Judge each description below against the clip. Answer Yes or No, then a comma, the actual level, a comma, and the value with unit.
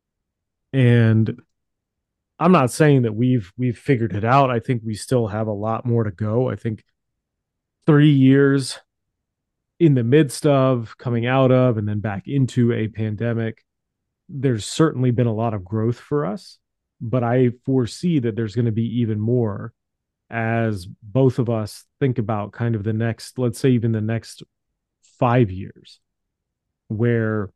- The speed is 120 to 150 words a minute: No, average, 160 wpm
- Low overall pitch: Yes, low, 120 Hz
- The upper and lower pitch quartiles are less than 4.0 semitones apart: Yes, average, 2.8 semitones